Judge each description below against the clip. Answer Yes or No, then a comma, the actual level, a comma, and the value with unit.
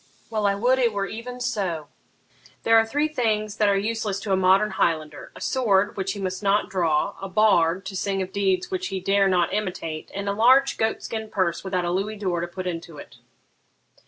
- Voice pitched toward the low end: No, high, 195 Hz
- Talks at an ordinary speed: No, fast, 215 wpm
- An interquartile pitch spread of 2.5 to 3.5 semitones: Yes, average, 2.8 semitones